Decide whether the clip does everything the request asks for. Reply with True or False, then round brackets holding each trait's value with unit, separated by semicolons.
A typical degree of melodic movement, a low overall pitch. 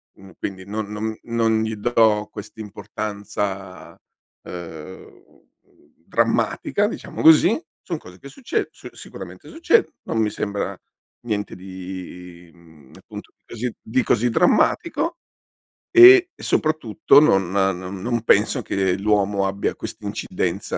True (3.6 semitones; 105 Hz)